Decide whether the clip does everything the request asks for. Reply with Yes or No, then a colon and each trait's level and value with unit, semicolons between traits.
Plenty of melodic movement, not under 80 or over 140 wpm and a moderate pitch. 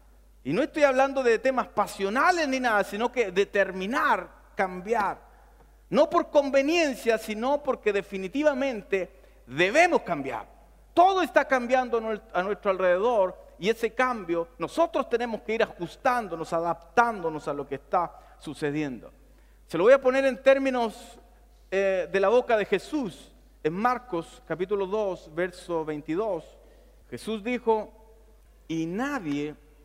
No: wide, 6.3 semitones; average, 130 wpm; high, 220 Hz